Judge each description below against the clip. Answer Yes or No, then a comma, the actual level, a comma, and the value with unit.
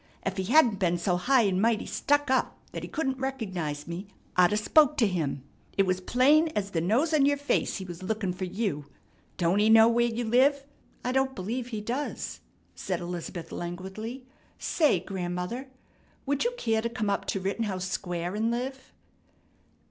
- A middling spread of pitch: No, wide, 5.9 semitones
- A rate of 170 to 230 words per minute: Yes, average, 185 wpm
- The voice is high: Yes, high, 215 Hz